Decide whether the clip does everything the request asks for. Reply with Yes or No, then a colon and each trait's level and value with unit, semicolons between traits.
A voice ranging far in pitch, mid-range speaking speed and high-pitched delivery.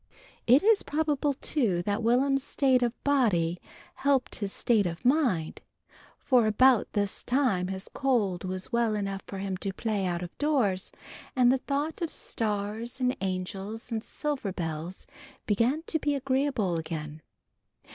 Yes: wide, 5.9 semitones; average, 150 wpm; high, 225 Hz